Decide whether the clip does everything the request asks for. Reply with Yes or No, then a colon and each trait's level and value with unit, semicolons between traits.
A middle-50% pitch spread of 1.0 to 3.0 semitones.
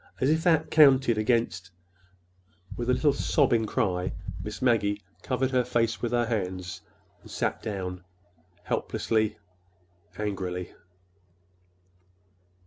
No: average, 4.6 semitones